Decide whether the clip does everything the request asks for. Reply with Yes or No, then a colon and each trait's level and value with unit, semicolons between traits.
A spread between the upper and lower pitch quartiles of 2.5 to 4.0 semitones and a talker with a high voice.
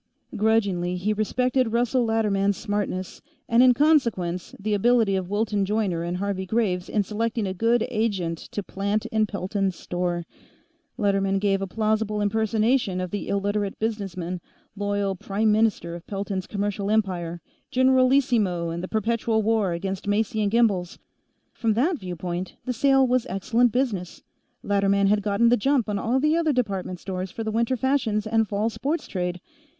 Yes: average, 3.0 semitones; high, 205 Hz